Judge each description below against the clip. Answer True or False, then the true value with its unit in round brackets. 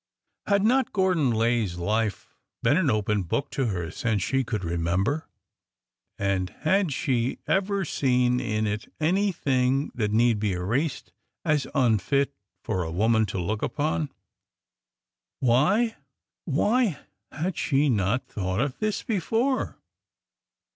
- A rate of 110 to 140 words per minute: True (135 wpm)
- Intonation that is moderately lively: False (7.2 semitones)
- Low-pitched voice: True (125 Hz)